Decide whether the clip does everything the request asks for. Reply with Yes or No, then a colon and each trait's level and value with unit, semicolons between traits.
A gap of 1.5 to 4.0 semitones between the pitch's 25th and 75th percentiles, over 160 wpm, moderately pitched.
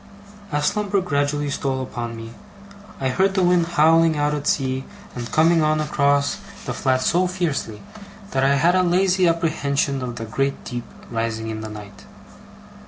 No: average, 4.6 semitones; average, 170 wpm; medium, 145 Hz